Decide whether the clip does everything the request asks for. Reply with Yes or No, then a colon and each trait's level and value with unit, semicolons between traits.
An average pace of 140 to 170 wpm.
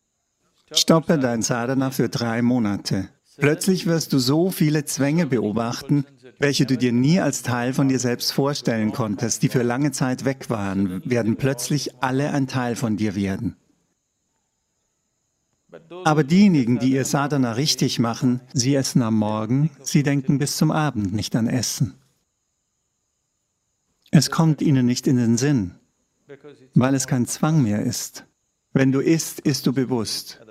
Yes: average, 150 wpm